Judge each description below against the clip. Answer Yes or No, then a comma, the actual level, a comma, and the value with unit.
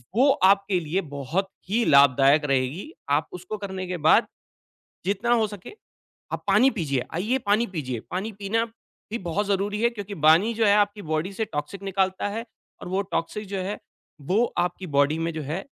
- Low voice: No, high, 190 Hz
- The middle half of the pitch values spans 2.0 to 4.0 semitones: No, average, 4.8 semitones